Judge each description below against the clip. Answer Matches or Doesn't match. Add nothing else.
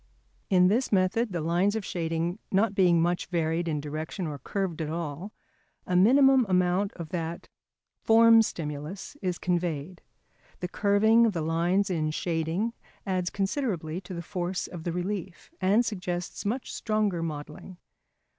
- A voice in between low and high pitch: Matches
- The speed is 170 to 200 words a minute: Doesn't match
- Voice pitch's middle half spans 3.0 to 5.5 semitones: Matches